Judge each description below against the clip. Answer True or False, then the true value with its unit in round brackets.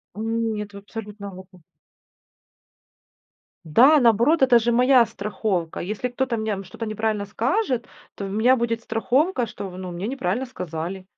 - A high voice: True (220 Hz)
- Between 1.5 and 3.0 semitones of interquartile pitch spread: False (3.6 semitones)